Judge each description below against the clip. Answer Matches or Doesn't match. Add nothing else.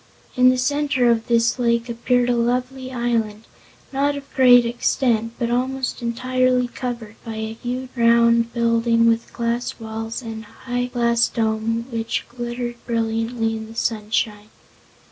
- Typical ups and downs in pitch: Doesn't match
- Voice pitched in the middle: Doesn't match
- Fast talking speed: Doesn't match